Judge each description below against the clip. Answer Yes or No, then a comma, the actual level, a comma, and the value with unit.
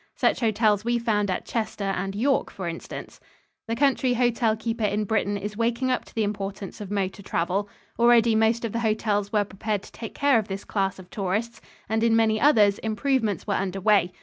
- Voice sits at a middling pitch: No, high, 215 Hz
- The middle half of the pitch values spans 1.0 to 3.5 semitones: Yes, narrow, 2.5 semitones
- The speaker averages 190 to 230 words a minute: Yes, average, 200 wpm